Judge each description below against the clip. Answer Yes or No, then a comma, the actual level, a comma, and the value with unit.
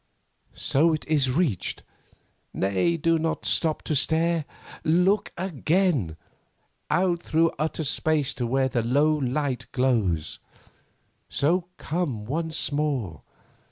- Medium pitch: Yes, medium, 150 Hz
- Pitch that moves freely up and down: No, average, 4.3 semitones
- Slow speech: Yes, slow, 115 wpm